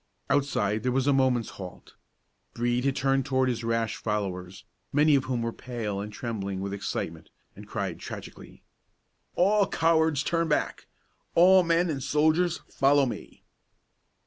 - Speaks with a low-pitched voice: Yes, low, 130 Hz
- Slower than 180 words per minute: Yes, average, 145 wpm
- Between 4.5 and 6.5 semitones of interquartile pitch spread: Yes, average, 5.0 semitones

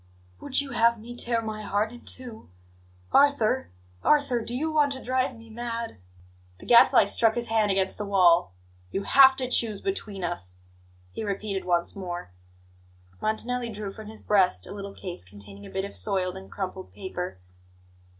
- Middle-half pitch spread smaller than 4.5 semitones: Yes, average, 4.1 semitones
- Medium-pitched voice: No, high, 215 Hz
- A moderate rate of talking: Yes, average, 170 wpm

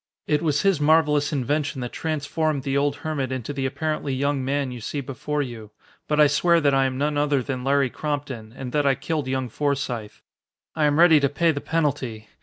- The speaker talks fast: Yes, fast, 210 wpm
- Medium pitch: Yes, medium, 145 Hz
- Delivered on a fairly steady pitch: Yes, narrow, 2.2 semitones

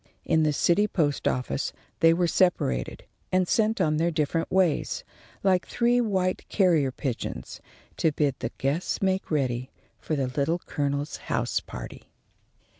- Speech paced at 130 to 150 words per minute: Yes, average, 145 wpm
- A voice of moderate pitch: Yes, medium, 160 Hz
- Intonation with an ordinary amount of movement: Yes, average, 4.5 semitones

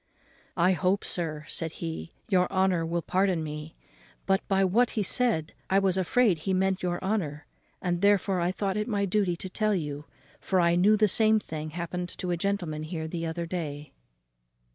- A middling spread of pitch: Yes, average, 3.0 semitones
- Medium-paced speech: Yes, average, 185 wpm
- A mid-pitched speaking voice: Yes, medium, 180 Hz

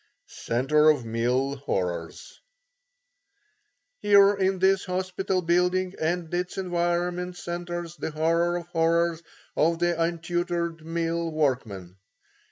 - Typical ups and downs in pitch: No, narrow, 2.3 semitones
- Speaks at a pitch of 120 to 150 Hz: No, medium, 170 Hz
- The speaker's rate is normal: No, slow, 105 wpm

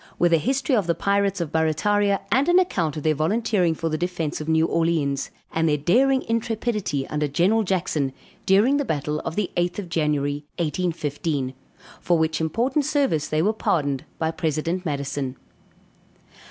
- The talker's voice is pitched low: No, medium, 165 Hz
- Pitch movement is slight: No, average, 5.2 semitones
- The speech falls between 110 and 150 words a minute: No, average, 165 wpm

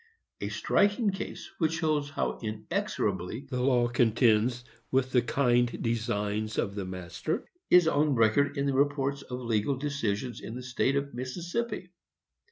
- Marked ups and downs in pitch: No, average, 4.0 semitones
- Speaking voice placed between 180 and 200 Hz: No, low, 125 Hz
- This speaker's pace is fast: No, average, 150 wpm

